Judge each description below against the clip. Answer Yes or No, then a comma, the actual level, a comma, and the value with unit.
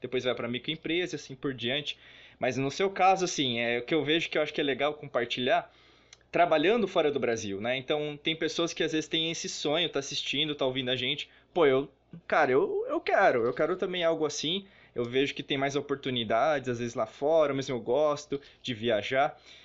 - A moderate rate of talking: No, fast, 215 wpm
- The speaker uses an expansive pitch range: No, average, 4.2 semitones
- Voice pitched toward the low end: No, medium, 145 Hz